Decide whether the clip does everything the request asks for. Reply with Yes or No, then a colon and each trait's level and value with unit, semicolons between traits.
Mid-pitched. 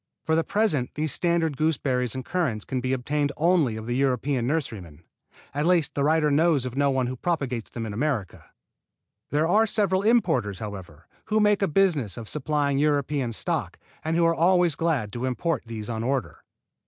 Yes: medium, 145 Hz